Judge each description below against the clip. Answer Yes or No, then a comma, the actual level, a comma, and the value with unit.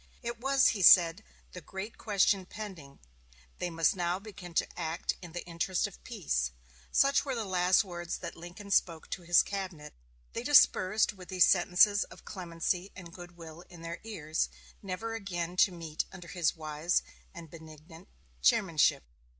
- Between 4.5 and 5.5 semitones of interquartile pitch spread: No, average, 2.9 semitones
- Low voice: No, medium, 175 Hz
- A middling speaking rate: Yes, average, 165 wpm